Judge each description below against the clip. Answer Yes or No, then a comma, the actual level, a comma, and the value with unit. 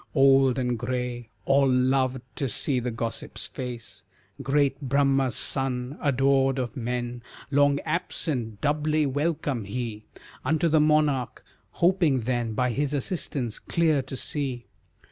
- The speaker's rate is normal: No, slow, 125 wpm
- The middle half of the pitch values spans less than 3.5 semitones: Yes, narrow, 2.6 semitones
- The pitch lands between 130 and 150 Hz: Yes, low, 135 Hz